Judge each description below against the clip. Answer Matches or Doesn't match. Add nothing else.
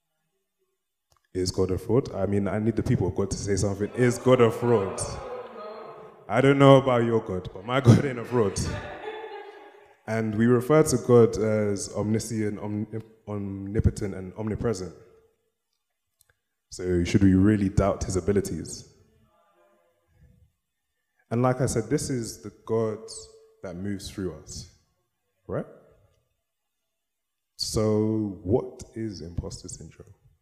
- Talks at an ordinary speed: Doesn't match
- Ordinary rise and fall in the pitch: Matches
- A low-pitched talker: Matches